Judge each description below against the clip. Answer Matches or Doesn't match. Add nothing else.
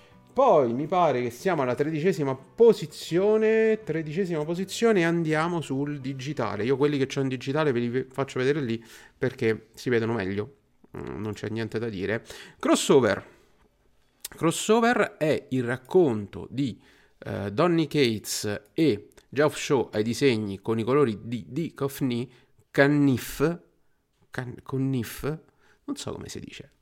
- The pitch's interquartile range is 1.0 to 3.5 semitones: Doesn't match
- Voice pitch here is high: Doesn't match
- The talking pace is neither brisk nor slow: Matches